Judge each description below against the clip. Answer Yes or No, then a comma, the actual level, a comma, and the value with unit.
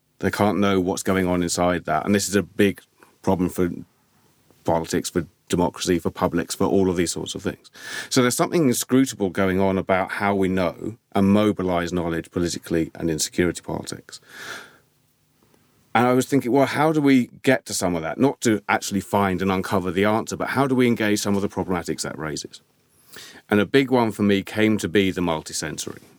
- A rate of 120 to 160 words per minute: No, average, 200 wpm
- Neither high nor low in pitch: No, very low, 95 Hz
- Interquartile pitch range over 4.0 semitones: No, average, 3.0 semitones